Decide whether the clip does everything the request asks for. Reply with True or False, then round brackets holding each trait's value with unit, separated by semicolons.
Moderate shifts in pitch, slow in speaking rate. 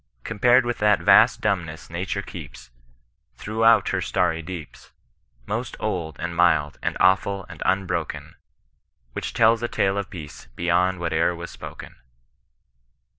True (4.0 semitones; 130 wpm)